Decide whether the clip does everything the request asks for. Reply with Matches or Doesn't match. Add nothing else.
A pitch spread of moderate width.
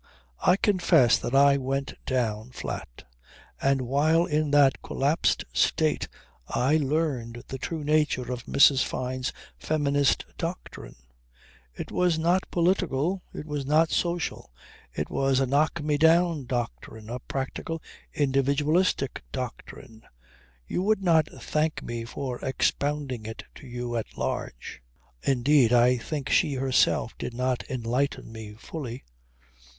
Matches